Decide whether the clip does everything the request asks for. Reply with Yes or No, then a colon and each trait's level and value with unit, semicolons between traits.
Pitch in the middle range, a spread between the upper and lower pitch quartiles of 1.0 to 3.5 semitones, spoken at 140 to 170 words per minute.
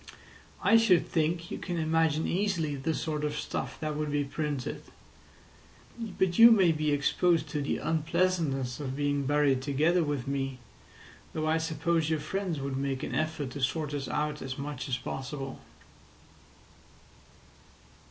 Yes: medium, 150 Hz; average, 2.7 semitones; average, 150 wpm